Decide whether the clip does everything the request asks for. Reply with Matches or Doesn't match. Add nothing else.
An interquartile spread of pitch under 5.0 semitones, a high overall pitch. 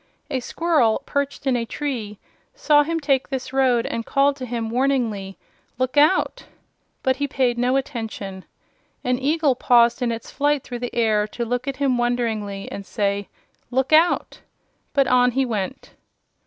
Matches